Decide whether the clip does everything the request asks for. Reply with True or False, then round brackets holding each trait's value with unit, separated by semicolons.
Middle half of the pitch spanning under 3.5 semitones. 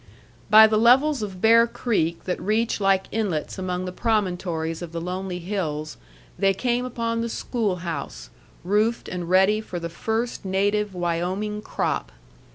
False (3.9 semitones)